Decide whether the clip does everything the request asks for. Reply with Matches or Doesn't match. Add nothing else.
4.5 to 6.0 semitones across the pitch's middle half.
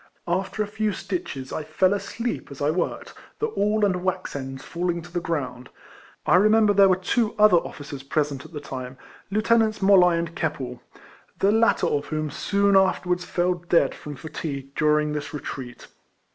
Matches